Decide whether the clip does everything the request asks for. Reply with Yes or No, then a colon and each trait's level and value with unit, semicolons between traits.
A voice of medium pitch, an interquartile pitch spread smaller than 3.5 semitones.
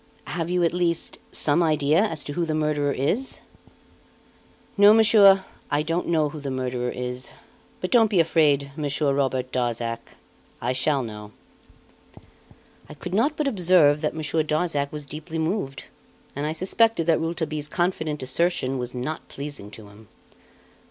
No: medium, 155 Hz; average, 4.1 semitones